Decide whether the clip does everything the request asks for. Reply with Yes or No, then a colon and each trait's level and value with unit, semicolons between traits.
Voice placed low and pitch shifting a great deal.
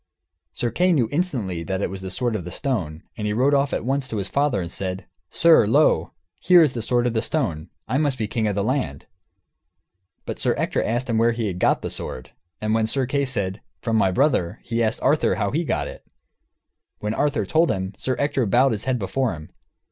Yes: low, 115 Hz; wide, 5.7 semitones